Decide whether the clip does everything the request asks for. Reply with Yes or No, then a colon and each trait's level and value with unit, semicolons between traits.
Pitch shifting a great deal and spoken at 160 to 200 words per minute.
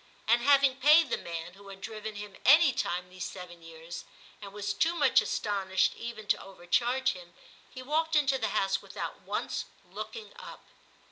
Yes: wide, 6.3 semitones; average, 175 wpm